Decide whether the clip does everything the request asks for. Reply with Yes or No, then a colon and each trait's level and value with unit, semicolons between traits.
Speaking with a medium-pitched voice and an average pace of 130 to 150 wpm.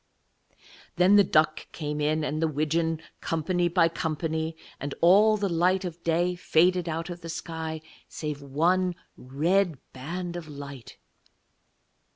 Yes: medium, 165 Hz; average, 140 wpm